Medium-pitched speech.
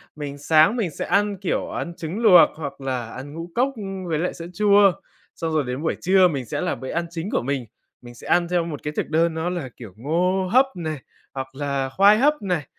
Yes: medium, 165 Hz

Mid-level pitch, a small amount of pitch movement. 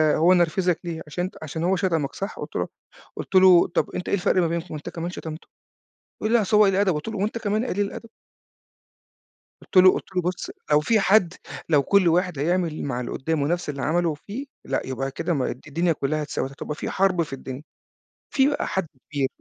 No: medium, 175 Hz; average, 4.1 semitones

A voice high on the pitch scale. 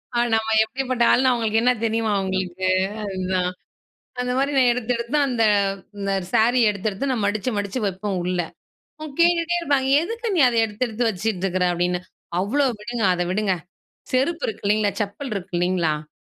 Yes: high, 220 Hz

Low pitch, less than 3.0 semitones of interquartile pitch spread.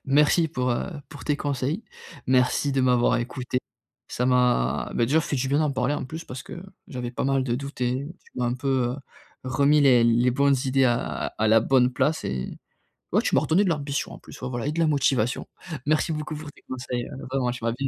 Yes: low, 130 Hz; narrow, 2.6 semitones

